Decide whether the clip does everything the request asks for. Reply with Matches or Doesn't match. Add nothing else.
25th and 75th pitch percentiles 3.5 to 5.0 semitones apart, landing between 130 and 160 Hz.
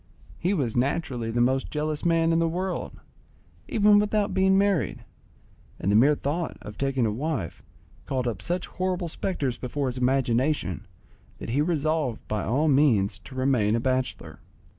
Doesn't match